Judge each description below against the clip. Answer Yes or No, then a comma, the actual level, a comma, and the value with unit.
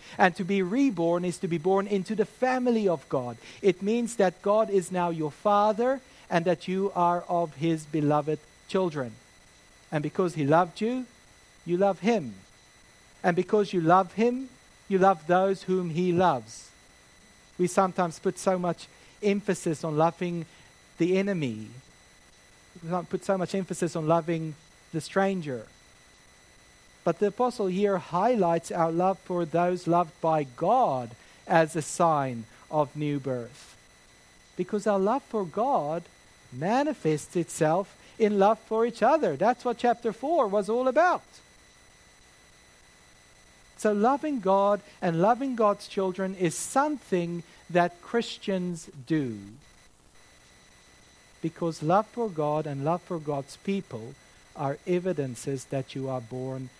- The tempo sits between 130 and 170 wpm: Yes, average, 140 wpm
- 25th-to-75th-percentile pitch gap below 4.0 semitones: No, average, 5.1 semitones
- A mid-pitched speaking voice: Yes, medium, 175 Hz